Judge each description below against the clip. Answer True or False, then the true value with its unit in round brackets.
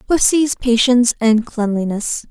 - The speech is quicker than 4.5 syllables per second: False (4.3 syllables/s)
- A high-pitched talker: True (235 Hz)